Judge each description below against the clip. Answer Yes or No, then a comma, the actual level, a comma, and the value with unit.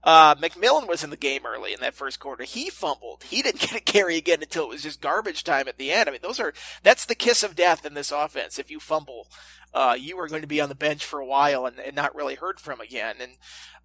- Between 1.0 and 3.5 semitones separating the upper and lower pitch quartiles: Yes, average, 2.8 semitones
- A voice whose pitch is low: No, medium, 155 Hz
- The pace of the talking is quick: Yes, fast, 270 wpm